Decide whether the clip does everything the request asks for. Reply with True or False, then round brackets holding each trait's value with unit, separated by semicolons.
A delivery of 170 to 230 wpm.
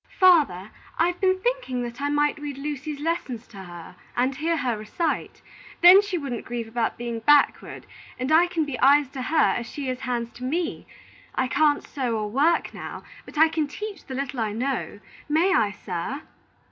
True (190 wpm)